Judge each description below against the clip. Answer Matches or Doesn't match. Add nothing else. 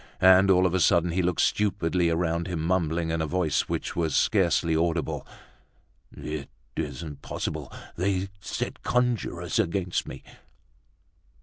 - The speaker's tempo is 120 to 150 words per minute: Matches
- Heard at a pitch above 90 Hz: Doesn't match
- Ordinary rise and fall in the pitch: Doesn't match